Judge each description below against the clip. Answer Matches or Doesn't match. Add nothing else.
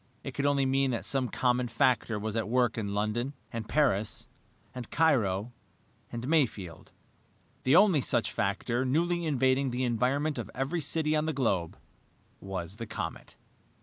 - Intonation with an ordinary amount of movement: Matches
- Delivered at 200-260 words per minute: Doesn't match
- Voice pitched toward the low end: Matches